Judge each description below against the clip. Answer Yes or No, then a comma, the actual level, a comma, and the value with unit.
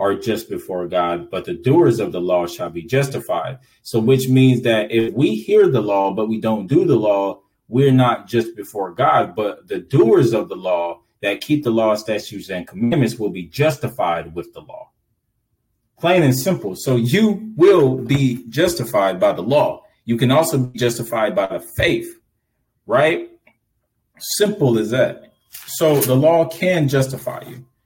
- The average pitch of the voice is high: No, low, 125 Hz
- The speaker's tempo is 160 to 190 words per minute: Yes, average, 175 wpm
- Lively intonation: Yes, wide, 5.8 semitones